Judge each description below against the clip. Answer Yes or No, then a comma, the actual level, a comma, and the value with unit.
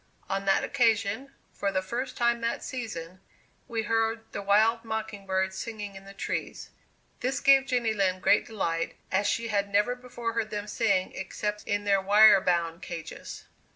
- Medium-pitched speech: No, high, 210 Hz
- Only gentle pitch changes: No, average, 3.0 semitones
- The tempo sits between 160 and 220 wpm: Yes, average, 170 wpm